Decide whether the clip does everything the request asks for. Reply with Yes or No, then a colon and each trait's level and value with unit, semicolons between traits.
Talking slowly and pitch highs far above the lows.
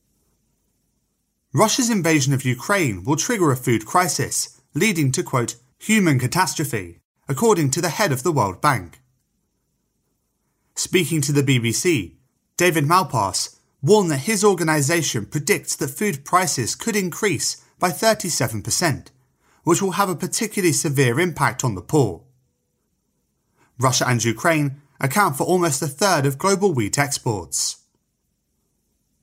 Yes: slow, 125 wpm; wide, 6.1 semitones